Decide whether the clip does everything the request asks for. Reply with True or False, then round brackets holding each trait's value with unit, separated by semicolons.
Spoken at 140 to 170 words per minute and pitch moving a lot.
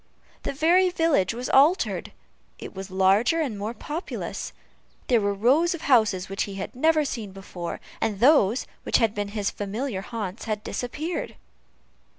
True (160 wpm; 6.6 semitones)